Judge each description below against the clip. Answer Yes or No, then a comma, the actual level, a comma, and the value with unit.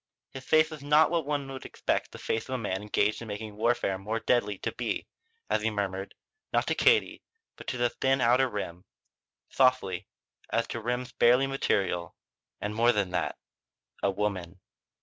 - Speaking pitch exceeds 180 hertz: No, low, 115 Hz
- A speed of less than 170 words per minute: No, average, 180 wpm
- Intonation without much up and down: No, average, 4.6 semitones